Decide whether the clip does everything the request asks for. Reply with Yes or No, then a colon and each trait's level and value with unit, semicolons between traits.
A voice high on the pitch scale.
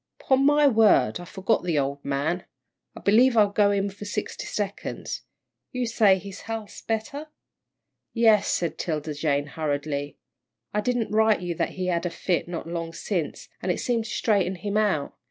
Yes: high, 195 Hz